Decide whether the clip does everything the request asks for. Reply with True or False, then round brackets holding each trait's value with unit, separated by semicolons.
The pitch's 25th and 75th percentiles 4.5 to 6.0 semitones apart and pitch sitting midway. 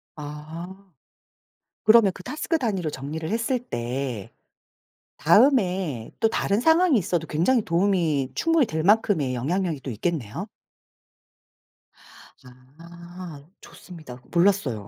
True (5.6 semitones; 175 Hz)